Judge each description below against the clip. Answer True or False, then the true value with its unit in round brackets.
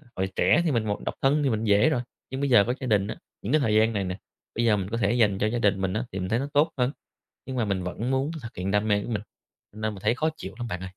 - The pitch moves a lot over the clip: False (3.8 semitones)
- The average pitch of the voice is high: False (110 Hz)